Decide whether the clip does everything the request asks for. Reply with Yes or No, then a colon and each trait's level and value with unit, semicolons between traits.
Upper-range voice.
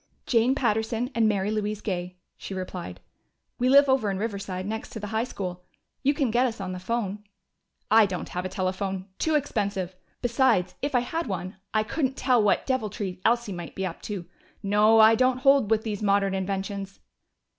Yes: high, 210 Hz